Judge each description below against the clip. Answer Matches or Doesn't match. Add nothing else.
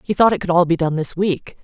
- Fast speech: Matches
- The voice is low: Doesn't match